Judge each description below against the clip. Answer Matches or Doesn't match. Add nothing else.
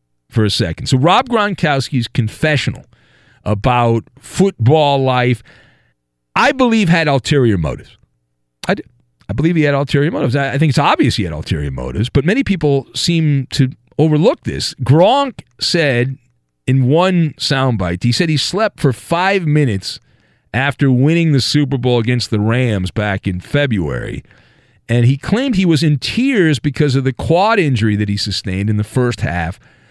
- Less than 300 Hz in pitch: Matches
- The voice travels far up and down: Matches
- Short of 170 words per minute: Matches